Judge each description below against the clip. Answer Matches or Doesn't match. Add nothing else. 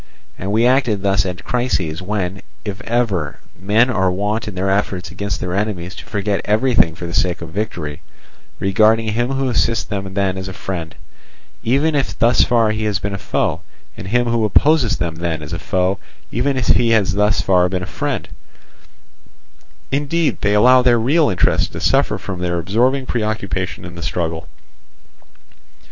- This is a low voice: Matches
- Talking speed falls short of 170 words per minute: Doesn't match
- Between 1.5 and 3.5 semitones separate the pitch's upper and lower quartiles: Doesn't match